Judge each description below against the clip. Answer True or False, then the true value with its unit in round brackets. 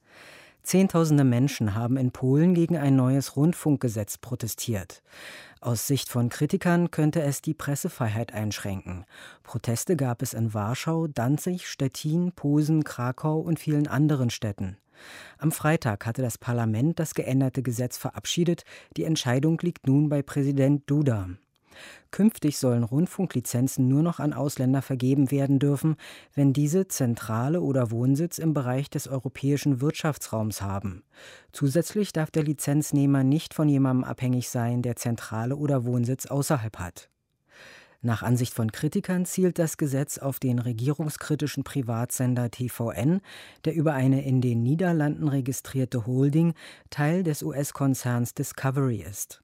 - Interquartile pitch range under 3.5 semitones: False (4.0 semitones)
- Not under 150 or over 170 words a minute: False (130 wpm)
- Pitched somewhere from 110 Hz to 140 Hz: True (135 Hz)